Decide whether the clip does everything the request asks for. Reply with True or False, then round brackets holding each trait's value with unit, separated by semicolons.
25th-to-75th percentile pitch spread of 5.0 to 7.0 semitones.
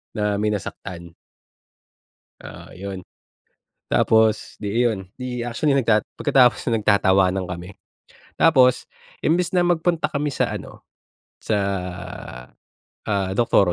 True (5.4 semitones)